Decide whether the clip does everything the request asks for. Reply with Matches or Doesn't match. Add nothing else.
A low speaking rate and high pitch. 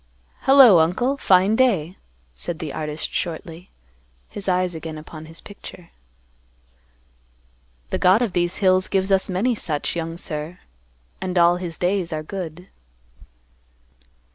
Doesn't match